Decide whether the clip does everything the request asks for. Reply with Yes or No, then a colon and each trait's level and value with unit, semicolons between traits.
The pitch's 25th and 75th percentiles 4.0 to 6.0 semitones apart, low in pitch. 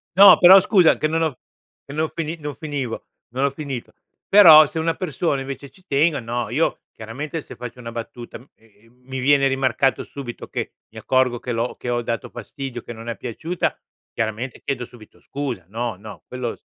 Yes: average, 4.4 semitones; low, 130 Hz